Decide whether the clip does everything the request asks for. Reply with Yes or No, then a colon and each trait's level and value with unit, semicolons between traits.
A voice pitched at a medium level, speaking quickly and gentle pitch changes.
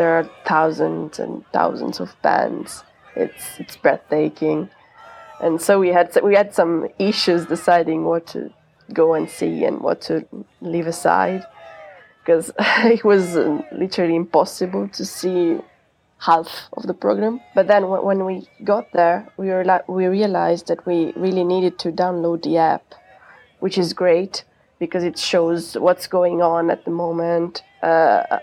No: medium, 175 Hz; average, 150 wpm; narrow, 2.2 semitones